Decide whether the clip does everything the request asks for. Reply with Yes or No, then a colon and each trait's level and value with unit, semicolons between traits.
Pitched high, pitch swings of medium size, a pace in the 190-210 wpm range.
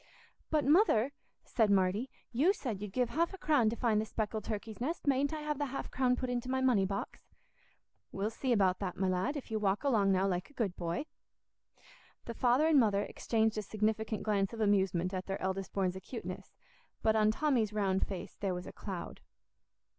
Yes: high, 220 Hz; average, 4.7 semitones; average, 200 wpm